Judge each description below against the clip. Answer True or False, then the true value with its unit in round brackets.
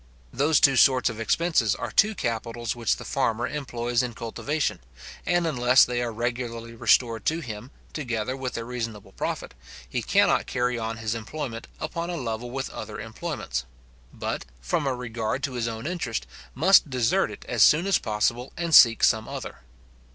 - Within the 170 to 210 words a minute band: True (175 wpm)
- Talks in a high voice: False (120 Hz)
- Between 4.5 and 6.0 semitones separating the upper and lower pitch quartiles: False (3.3 semitones)